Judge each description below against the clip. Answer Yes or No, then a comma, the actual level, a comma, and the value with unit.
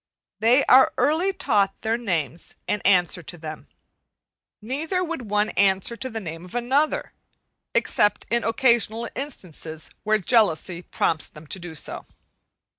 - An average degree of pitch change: No, wide, 6.0 semitones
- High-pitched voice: Yes, high, 215 Hz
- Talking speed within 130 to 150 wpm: Yes, average, 140 wpm